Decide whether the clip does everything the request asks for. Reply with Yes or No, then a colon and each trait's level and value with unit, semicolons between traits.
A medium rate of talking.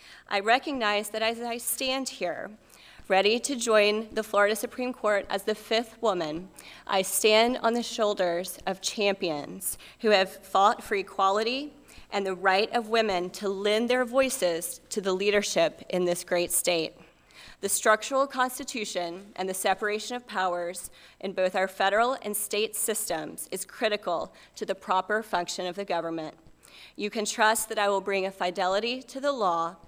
Yes: average, 165 wpm